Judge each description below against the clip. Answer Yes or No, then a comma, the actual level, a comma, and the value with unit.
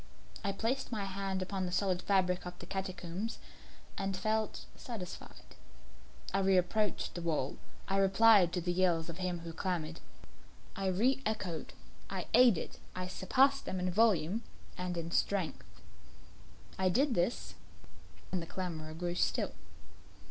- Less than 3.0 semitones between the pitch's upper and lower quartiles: Yes, narrow, 2.5 semitones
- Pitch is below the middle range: No, medium, 185 Hz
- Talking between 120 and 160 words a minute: Yes, average, 140 wpm